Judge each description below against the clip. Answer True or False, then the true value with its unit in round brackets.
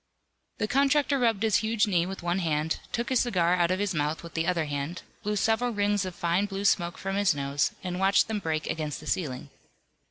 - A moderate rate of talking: False (220 wpm)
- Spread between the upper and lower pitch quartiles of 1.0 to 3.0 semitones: False (4.1 semitones)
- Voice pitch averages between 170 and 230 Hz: True (185 Hz)